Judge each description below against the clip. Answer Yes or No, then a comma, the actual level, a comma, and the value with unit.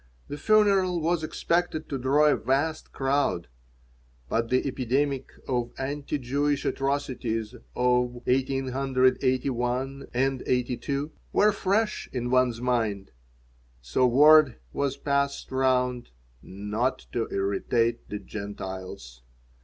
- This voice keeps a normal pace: No, slow, 105 wpm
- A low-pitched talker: Yes, low, 130 Hz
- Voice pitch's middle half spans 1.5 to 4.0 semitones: Yes, average, 2.8 semitones